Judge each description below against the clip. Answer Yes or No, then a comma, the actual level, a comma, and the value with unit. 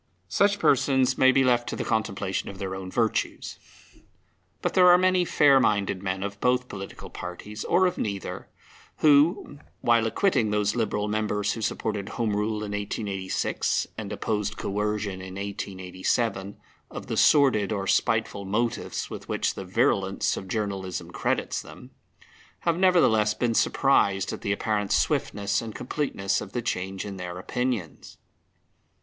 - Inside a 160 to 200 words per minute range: No, average, 150 wpm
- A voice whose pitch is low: Yes, low, 105 Hz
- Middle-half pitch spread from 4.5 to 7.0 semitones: No, average, 4.0 semitones